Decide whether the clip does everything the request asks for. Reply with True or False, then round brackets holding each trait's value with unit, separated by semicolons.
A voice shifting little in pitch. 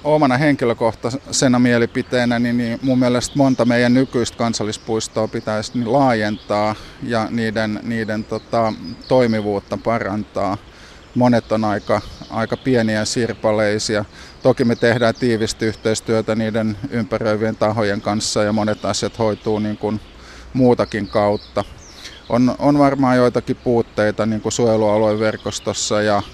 True (2.3 semitones)